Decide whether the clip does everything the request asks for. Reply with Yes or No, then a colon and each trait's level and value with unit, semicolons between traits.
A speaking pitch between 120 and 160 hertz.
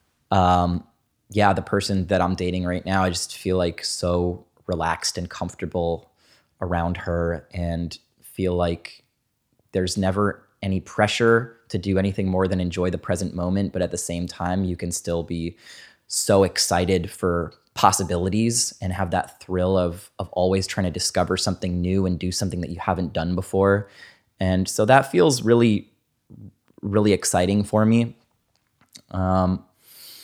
No: very low, 95 Hz